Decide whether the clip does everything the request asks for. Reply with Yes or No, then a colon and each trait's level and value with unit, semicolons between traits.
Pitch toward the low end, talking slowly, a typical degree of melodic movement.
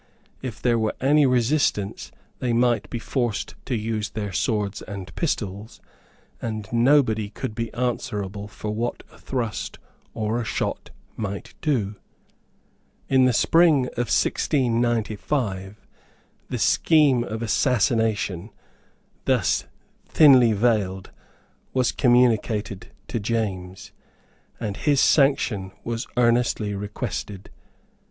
Yes: low, 115 Hz; slow, 110 wpm; average, 3.2 semitones